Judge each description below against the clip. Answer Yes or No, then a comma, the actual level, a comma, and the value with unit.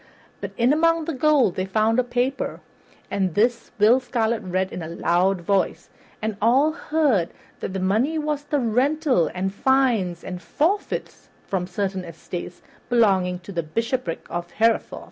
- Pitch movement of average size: No, wide, 6.1 semitones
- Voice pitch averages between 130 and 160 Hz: No, high, 220 Hz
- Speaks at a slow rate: No, average, 160 wpm